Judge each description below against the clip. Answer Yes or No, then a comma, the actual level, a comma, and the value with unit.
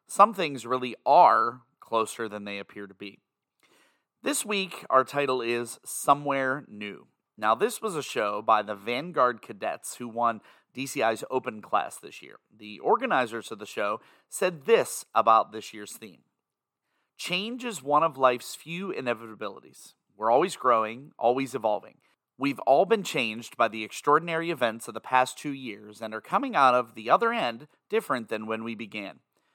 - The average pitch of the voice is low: Yes, low, 120 Hz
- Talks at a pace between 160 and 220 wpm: Yes, average, 165 wpm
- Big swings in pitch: No, average, 4.5 semitones